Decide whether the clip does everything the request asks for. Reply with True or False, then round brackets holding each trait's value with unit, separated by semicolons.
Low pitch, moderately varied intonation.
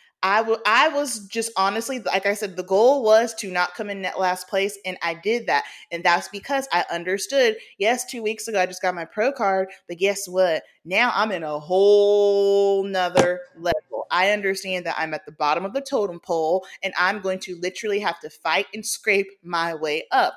False (195 Hz; 3.1 semitones)